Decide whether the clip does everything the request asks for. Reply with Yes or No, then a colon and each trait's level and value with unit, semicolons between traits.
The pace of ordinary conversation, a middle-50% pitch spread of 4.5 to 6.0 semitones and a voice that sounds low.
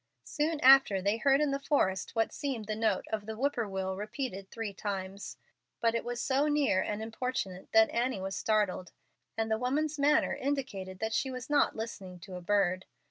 No: average, 190 wpm; wide, 5.6 semitones; high, 220 Hz